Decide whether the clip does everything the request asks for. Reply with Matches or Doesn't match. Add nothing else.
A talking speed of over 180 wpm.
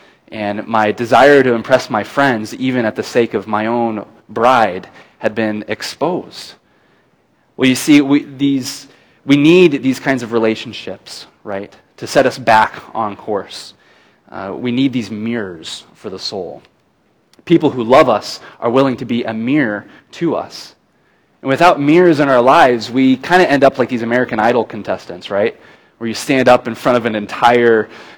Doesn't match